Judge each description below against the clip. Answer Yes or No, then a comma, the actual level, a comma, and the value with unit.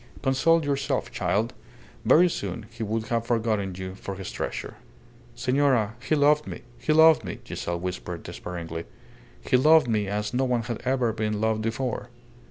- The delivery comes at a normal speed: Yes, average, 165 wpm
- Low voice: Yes, low, 115 Hz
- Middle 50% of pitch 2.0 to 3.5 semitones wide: No, average, 4.4 semitones